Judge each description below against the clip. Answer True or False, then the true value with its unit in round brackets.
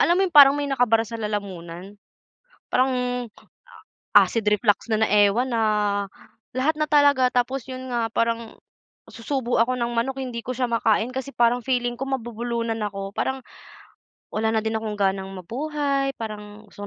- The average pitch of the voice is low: False (235 Hz)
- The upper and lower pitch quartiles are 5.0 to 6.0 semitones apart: False (3.3 semitones)